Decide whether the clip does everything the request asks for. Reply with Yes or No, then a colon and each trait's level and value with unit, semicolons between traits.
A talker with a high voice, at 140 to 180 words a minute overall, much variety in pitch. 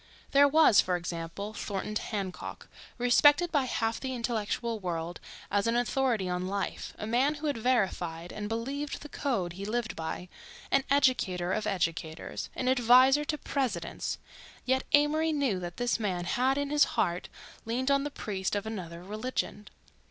Yes: high, 225 Hz; average, 160 wpm; wide, 6.2 semitones